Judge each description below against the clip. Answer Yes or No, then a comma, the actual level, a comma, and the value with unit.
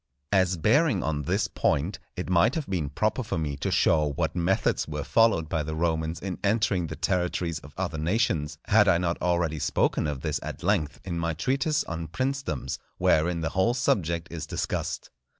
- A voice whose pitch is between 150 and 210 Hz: No, very low, 85 Hz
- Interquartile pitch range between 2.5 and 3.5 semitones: No, average, 4.0 semitones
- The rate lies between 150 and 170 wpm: No, average, 185 wpm